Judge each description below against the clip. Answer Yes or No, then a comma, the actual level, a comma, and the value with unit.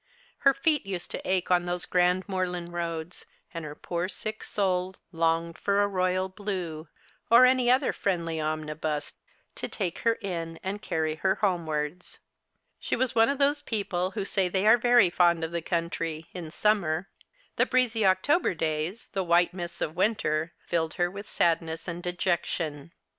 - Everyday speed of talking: Yes, average, 170 wpm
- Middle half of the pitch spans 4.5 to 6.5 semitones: No, average, 3.4 semitones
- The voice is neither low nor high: Yes, medium, 180 Hz